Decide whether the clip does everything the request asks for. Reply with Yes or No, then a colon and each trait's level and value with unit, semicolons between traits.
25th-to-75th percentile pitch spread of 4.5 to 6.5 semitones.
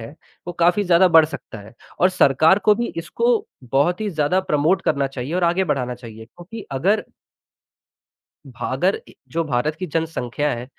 Yes: average, 5.3 semitones